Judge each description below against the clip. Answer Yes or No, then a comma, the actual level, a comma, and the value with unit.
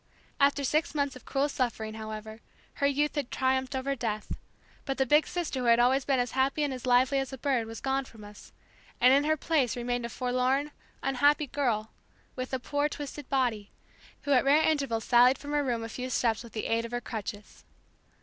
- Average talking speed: No, fast, 210 wpm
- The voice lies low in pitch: No, very high, 260 Hz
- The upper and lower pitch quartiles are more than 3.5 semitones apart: No, average, 3.1 semitones